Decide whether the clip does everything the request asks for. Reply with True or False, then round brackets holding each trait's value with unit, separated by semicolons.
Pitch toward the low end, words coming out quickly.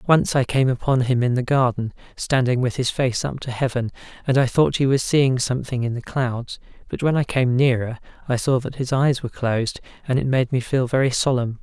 True (130 Hz; 225 wpm)